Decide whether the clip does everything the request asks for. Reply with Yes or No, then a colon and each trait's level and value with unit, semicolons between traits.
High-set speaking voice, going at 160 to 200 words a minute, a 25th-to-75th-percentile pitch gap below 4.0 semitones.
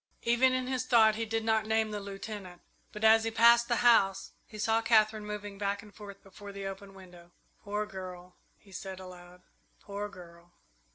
Yes: high, 205 Hz; average, 185 wpm; narrow, 2.5 semitones